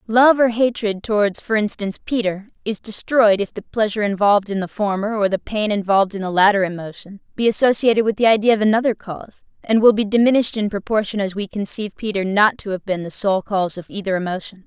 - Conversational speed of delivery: No, fast, 215 wpm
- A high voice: Yes, high, 205 Hz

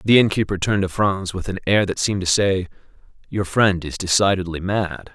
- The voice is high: No, very low, 95 Hz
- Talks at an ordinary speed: No, fast, 210 wpm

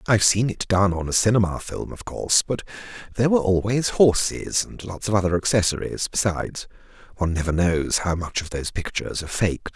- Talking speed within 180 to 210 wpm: Yes, average, 190 wpm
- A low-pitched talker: Yes, very low, 95 Hz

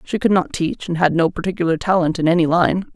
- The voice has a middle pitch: Yes, medium, 175 Hz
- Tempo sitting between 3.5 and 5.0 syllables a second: No, 6.2 syllables/s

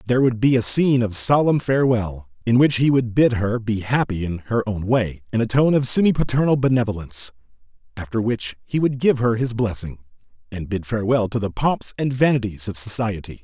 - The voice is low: Yes, low, 115 Hz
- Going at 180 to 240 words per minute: Yes, average, 200 wpm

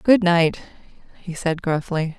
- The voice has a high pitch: No, medium, 175 Hz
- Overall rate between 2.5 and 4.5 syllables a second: Yes, 4.0 syllables/s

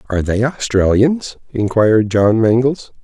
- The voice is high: No, low, 115 Hz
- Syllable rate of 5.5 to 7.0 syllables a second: No, 4.4 syllables/s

